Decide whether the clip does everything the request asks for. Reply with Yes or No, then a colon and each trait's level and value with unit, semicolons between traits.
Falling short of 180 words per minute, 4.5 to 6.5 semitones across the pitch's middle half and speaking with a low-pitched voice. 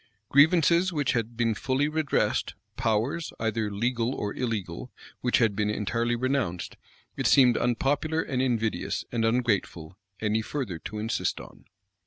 No: average, 140 wpm; average, 3.8 semitones; low, 120 Hz